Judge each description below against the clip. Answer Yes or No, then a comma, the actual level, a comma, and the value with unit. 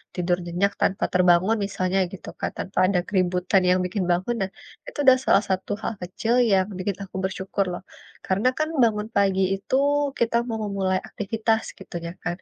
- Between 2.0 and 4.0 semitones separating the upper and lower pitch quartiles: Yes, narrow, 2.4 semitones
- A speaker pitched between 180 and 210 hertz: Yes, high, 190 Hz